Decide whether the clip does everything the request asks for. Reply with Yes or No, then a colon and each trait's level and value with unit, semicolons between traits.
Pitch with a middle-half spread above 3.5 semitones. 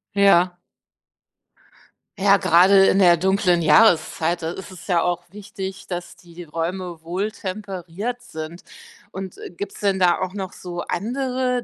No: narrow, 2.4 semitones